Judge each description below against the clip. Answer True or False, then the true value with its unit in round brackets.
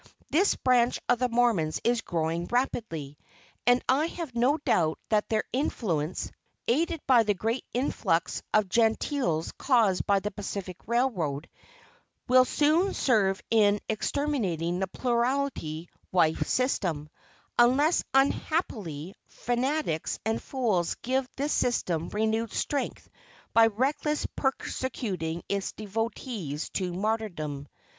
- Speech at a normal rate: False (115 wpm)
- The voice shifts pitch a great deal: True (6.4 semitones)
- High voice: True (225 Hz)